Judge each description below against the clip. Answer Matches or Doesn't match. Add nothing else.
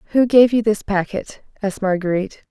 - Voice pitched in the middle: Doesn't match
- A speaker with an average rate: Matches